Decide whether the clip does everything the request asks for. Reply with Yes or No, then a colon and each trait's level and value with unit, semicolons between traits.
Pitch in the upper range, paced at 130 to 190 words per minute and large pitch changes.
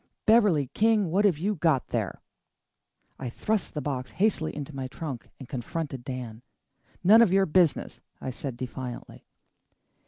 No: medium, 150 Hz; average, 150 wpm; wide, 7.0 semitones